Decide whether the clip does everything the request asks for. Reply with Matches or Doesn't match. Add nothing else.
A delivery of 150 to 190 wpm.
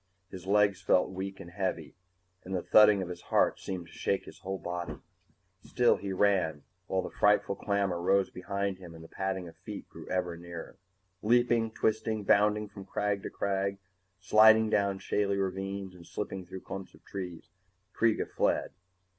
Matches